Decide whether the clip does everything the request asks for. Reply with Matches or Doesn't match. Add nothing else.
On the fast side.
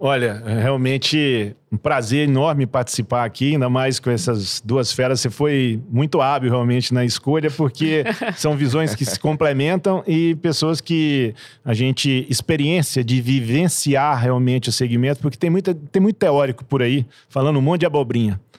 Doesn't match